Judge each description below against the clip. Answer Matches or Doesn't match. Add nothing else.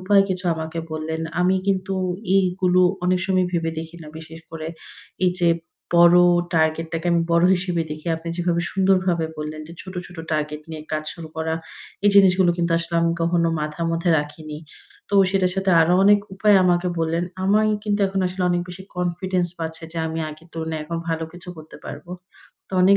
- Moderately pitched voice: Matches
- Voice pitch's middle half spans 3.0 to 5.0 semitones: Doesn't match